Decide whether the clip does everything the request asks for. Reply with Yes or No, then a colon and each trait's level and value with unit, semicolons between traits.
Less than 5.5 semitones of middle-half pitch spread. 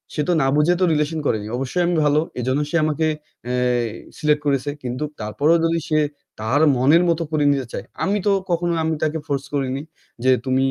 Yes: average, 3.6 semitones